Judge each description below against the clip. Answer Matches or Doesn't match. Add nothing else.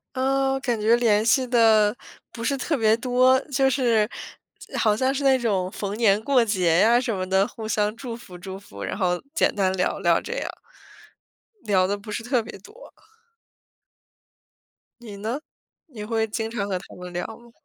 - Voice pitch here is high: Matches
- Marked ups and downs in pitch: Doesn't match